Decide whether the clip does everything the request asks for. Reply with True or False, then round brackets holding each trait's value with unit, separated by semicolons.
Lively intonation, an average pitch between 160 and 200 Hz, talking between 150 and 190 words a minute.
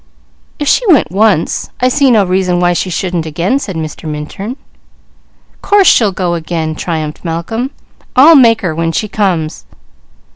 True (5.9 semitones; 185 Hz; 155 wpm)